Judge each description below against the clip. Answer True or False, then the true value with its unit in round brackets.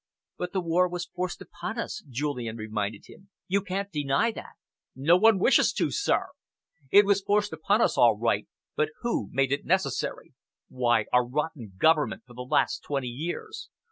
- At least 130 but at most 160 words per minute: False (170 wpm)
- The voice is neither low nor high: True (155 Hz)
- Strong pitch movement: True (7.9 semitones)